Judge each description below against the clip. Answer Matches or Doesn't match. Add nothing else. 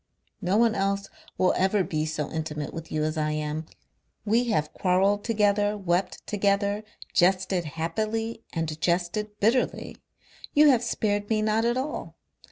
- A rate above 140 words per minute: Matches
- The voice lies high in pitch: Matches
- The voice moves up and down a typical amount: Matches